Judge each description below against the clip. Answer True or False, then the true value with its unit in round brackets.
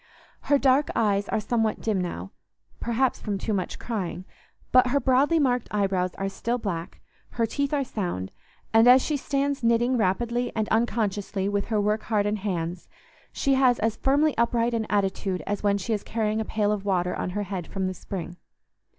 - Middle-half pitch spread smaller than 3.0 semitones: False (3.9 semitones)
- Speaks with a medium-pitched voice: False (215 Hz)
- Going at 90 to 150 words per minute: False (180 wpm)